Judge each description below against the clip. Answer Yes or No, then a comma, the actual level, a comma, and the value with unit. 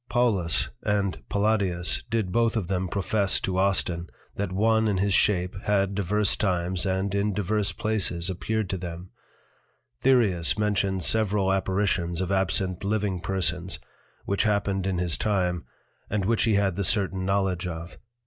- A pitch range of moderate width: No, narrow, 2.3 semitones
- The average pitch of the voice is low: Yes, very low, 95 Hz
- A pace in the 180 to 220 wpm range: No, average, 150 wpm